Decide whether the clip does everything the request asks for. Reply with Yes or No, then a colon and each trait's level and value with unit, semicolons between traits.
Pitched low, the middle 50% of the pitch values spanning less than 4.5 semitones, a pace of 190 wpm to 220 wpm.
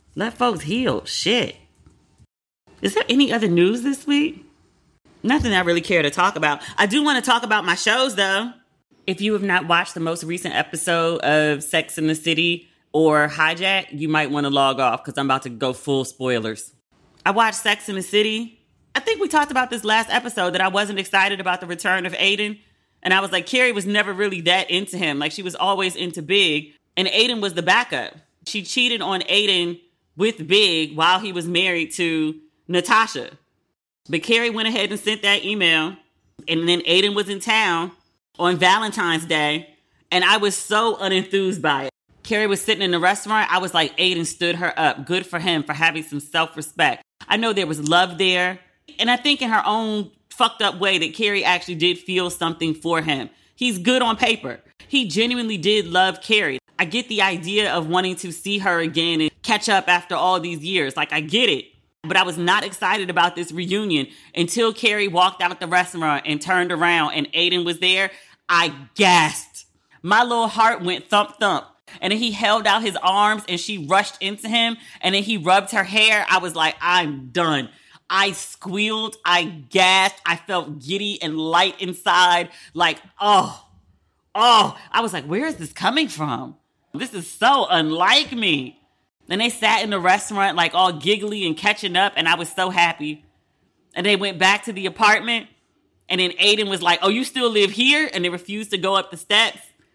No: medium, 185 Hz; average, 3.7 semitones; average, 200 wpm